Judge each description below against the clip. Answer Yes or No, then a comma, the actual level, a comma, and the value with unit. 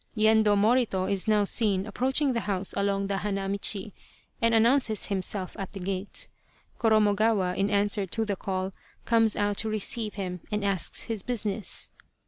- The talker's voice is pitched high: Yes, high, 205 Hz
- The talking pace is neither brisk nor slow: Yes, average, 160 wpm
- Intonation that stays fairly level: Yes, narrow, 2.1 semitones